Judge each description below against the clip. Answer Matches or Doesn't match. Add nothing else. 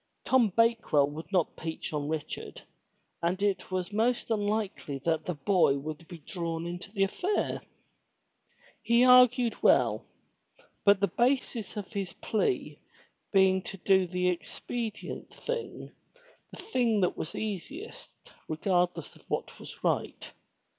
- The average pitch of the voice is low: Doesn't match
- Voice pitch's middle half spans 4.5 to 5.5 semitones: Matches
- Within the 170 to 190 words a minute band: Doesn't match